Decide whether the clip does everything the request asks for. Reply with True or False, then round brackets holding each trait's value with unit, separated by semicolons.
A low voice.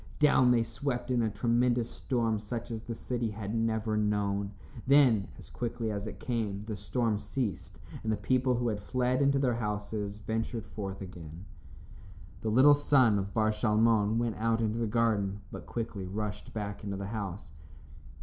True (110 Hz)